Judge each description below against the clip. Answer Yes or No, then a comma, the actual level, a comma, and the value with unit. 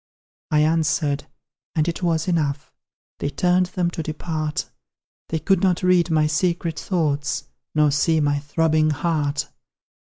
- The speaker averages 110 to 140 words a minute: Yes, slow, 135 wpm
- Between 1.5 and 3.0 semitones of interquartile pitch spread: Yes, narrow, 2.4 semitones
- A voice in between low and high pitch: Yes, medium, 155 Hz